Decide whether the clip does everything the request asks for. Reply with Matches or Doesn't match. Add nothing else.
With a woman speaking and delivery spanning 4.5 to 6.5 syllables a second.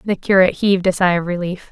Doesn't match